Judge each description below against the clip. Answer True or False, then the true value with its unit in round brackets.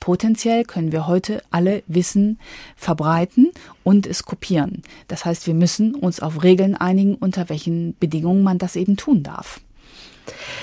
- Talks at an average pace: True (145 wpm)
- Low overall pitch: False (180 Hz)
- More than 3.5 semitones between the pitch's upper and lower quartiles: False (2.8 semitones)